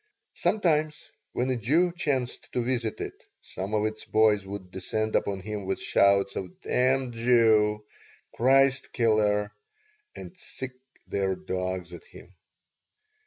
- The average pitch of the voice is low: Yes, low, 110 Hz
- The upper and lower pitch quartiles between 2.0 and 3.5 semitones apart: No, average, 4.4 semitones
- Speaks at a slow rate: Yes, slow, 130 wpm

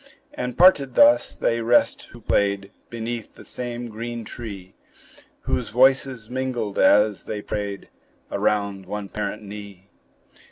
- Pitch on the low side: Yes, low, 110 Hz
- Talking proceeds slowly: Yes, slow, 125 wpm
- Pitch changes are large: No, average, 3.1 semitones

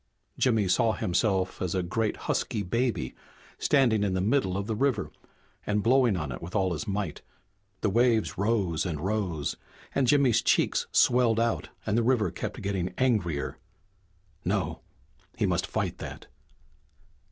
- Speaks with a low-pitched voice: Yes, low, 105 Hz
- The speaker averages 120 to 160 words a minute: Yes, average, 150 wpm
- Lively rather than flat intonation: No, average, 4.2 semitones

